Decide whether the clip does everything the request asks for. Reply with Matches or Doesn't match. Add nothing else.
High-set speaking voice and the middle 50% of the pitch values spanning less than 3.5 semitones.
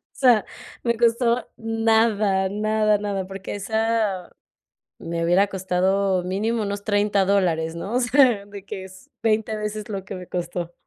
Matches